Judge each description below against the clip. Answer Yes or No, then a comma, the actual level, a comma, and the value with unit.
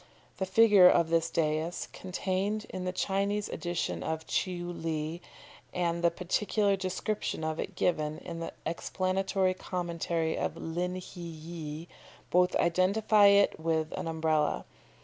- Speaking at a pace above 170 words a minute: No, slow, 135 wpm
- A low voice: No, medium, 175 Hz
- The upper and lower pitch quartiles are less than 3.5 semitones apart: Yes, narrow, 2.5 semitones